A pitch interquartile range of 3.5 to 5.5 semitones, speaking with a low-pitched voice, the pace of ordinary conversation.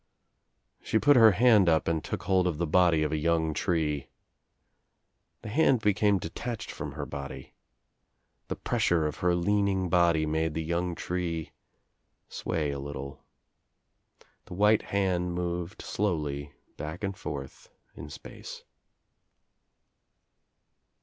No: average, 3.8 semitones; very low, 85 Hz; slow, 130 wpm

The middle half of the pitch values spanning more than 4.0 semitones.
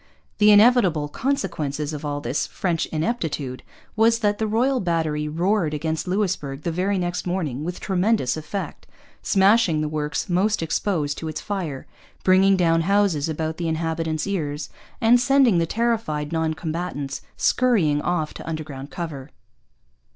Yes: average, 4.9 semitones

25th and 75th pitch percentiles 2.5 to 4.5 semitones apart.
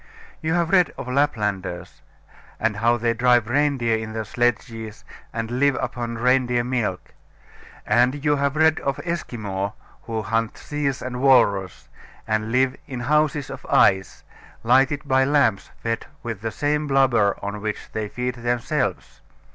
Yes: average, 3.8 semitones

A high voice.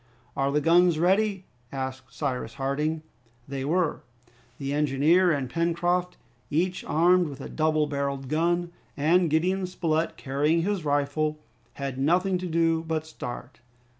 No: medium, 155 Hz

